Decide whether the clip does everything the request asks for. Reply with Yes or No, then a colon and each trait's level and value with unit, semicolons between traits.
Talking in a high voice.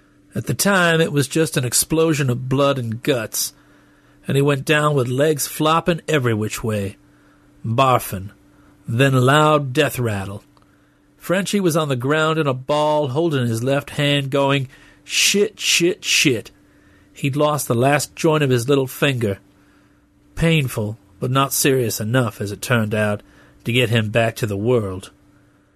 No: low, 135 Hz